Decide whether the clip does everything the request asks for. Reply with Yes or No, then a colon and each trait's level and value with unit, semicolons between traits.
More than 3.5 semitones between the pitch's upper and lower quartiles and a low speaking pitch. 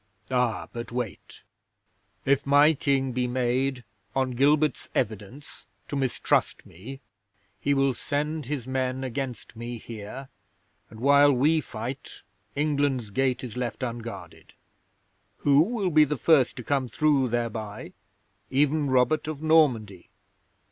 No: average, 3.1 semitones; low, 130 Hz